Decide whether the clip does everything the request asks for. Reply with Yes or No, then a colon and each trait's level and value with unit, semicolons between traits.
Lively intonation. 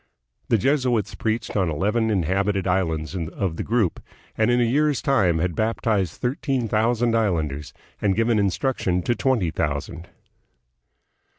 No: average, 5.0 semitones